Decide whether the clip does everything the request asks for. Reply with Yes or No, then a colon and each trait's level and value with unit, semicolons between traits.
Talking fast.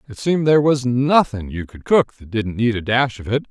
Yes: fast, 255 wpm